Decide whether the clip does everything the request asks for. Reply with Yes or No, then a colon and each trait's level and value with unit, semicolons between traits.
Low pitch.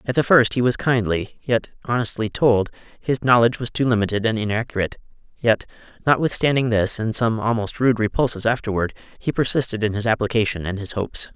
Yes: low, 115 Hz